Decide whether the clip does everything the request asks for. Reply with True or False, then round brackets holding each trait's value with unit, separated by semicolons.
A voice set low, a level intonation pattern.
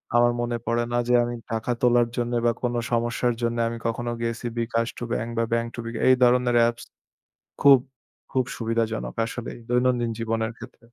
True (120 Hz; 0.8 semitones)